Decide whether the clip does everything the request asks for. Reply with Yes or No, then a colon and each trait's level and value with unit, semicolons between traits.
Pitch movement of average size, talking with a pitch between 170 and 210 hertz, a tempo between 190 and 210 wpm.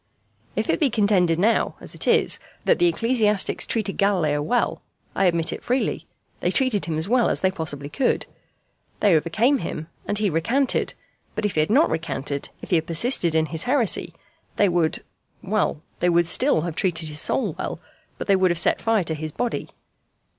No: wide, 5.9 semitones; medium, 185 Hz; average, 195 wpm